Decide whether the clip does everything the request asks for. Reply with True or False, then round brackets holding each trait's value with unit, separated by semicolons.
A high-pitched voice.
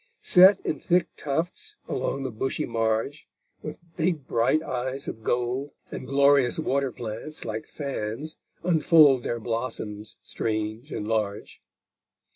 False (130 Hz)